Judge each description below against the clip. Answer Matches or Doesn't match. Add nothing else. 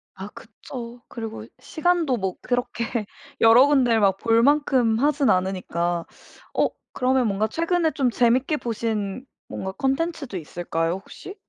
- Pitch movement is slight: Doesn't match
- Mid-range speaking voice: Doesn't match